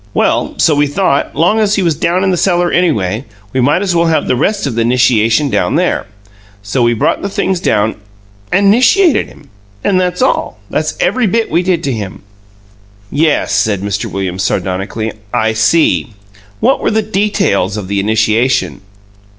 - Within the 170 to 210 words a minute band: Yes, average, 185 wpm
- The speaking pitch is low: No, medium, 145 Hz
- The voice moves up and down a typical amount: No, wide, 8.9 semitones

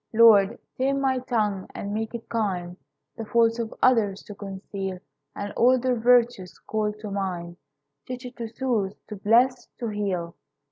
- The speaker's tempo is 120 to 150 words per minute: No, average, 160 wpm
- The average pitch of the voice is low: No, high, 220 Hz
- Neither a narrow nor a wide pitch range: Yes, average, 3.6 semitones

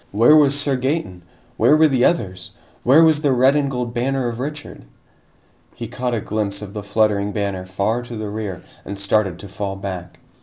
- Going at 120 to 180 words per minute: No, average, 195 wpm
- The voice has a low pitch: Yes, low, 115 Hz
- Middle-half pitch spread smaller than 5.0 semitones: No, average, 5.3 semitones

